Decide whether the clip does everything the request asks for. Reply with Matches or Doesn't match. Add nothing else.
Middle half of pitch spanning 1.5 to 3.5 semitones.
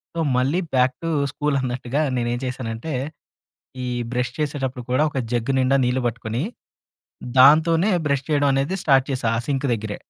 Matches